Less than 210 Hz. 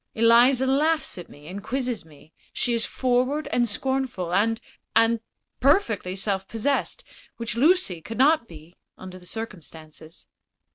No: high, 230 Hz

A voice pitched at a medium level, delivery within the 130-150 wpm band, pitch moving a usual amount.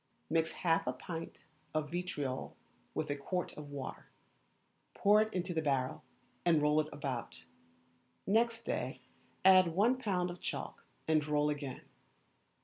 Yes: medium, 160 Hz; average, 140 wpm; average, 3.9 semitones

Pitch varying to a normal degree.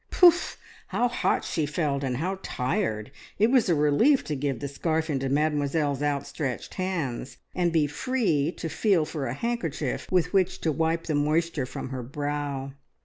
Yes: average, 3.8 semitones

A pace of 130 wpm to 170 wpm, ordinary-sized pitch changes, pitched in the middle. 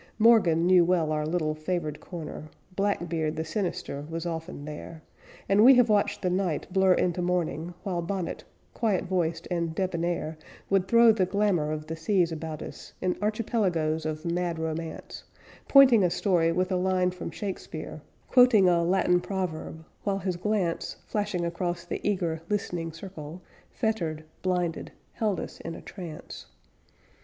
Yes: average, 155 wpm; average, 3.1 semitones; medium, 175 Hz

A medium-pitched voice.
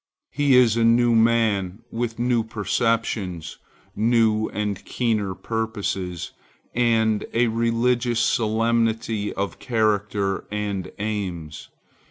No: low, 110 Hz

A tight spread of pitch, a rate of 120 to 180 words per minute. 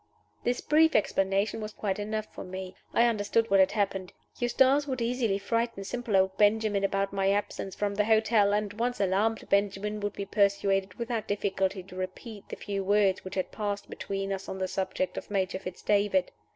No: narrow, 2.1 semitones; average, 190 wpm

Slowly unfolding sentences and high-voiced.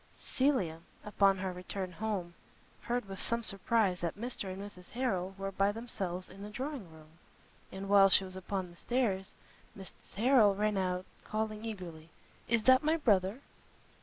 No: average, 165 wpm; high, 195 Hz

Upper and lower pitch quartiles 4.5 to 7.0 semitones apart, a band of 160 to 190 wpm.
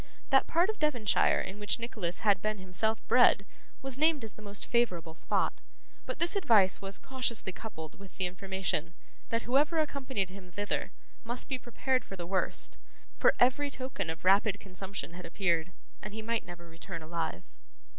Yes: average, 5.2 semitones; average, 175 wpm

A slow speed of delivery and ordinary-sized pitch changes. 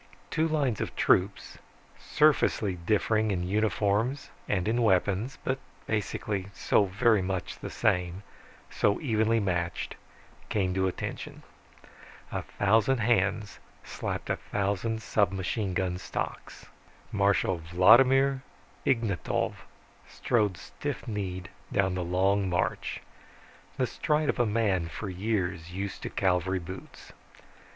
Yes: slow, 115 wpm; average, 3.4 semitones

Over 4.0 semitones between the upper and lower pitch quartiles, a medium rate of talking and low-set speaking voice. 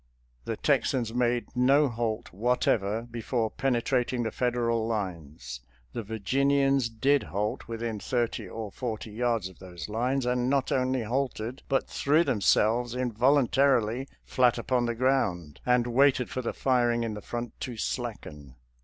No: average, 2.7 semitones; average, 150 wpm; low, 120 Hz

